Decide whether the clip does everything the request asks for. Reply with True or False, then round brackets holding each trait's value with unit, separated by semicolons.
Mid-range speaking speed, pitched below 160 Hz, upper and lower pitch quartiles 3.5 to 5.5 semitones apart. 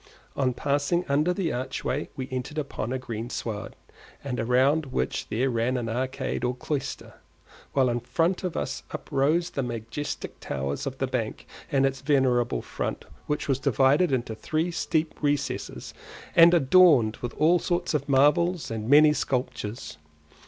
True (150 wpm; 135 Hz; 3.8 semitones)